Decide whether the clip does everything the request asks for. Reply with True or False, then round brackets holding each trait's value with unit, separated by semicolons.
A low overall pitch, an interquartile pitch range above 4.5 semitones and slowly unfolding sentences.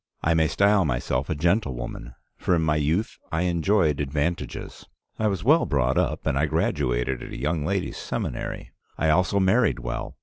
False (80 Hz; 5.2 semitones; 175 wpm)